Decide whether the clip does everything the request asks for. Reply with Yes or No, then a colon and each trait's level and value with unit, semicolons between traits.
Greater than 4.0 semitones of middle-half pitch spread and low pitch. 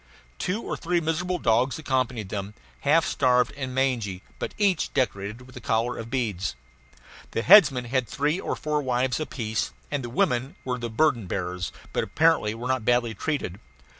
Yes: average, 4.6 semitones; low, 125 Hz